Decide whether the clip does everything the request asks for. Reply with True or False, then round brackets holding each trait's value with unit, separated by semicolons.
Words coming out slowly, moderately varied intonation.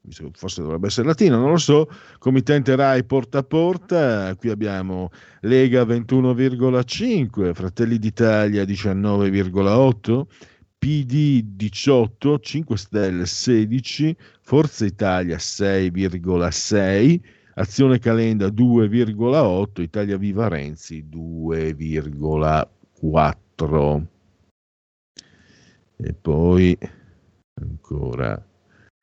False (75 wpm; 6.2 semitones)